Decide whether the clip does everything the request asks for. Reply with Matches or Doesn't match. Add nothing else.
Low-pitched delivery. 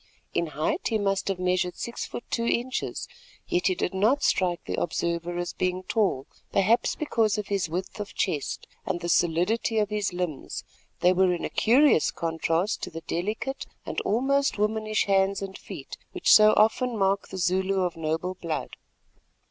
Doesn't match